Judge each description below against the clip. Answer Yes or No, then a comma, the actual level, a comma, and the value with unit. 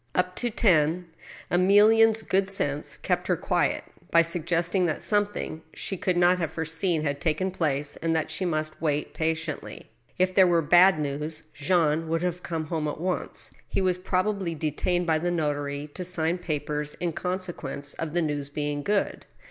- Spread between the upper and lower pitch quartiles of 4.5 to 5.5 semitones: No, average, 3.1 semitones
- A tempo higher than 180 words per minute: No, average, 175 wpm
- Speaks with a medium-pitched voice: Yes, medium, 165 Hz